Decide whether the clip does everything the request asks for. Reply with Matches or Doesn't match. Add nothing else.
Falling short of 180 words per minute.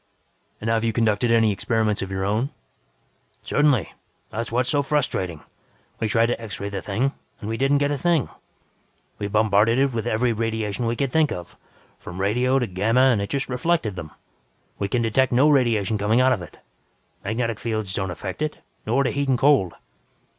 Doesn't match